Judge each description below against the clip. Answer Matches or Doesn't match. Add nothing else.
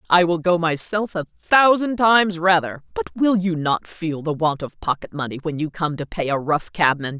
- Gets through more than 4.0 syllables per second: Matches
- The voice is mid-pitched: Matches